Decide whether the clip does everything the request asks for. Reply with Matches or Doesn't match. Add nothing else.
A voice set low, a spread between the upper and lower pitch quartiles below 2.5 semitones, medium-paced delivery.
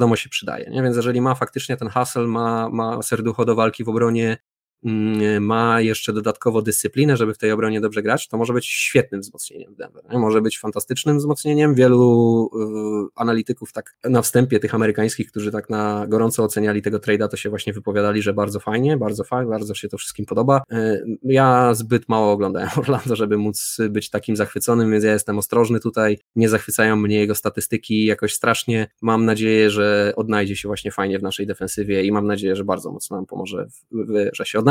Doesn't match